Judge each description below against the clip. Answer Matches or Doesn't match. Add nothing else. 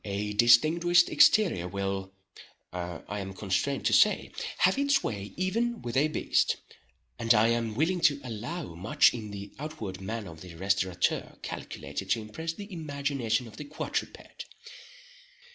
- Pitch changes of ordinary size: Doesn't match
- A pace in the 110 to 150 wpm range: Matches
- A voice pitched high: Doesn't match